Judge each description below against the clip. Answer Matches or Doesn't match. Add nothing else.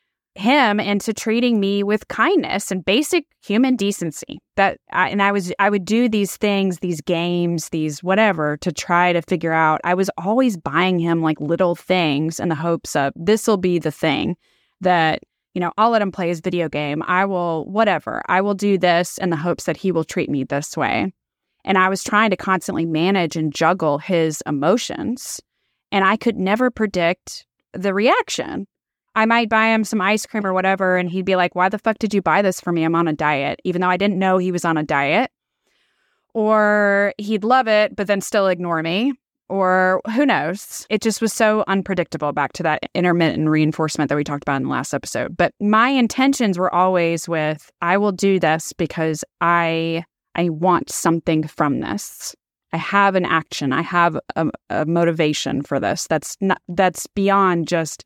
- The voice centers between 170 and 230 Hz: Matches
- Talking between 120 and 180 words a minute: Doesn't match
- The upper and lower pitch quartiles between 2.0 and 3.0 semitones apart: Doesn't match